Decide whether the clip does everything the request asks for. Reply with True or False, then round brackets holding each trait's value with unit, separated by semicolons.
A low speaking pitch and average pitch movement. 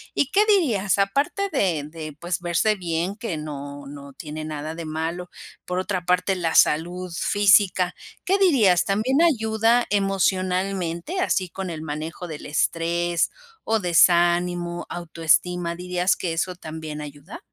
False (180 Hz; 3.3 semitones)